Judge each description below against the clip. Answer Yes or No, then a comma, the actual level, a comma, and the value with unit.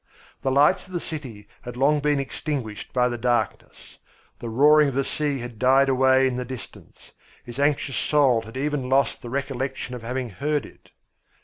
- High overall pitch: No, low, 130 Hz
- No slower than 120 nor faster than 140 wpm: No, average, 185 wpm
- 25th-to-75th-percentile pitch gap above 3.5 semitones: No, average, 2.7 semitones